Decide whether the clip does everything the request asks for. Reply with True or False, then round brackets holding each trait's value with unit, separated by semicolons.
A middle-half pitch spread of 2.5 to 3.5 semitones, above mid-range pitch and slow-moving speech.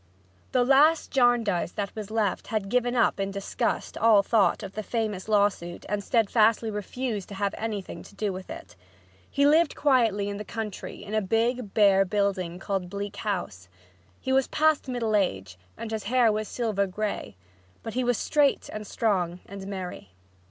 False (3.2 semitones; 210 Hz; 175 wpm)